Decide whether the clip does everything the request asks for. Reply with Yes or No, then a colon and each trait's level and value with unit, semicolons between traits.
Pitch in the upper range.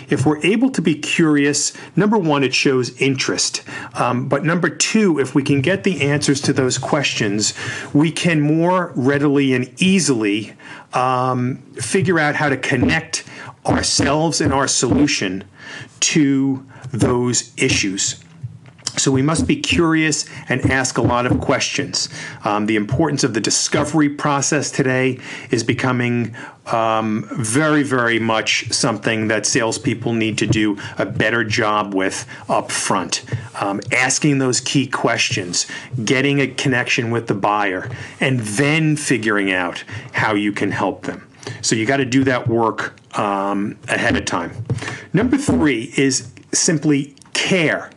No: low, 135 Hz